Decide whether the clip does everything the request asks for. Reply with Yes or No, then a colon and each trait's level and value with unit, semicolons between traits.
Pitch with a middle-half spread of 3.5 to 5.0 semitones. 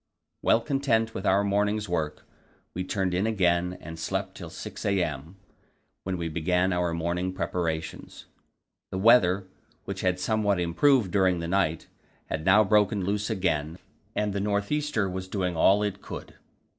No: average, 2.9 semitones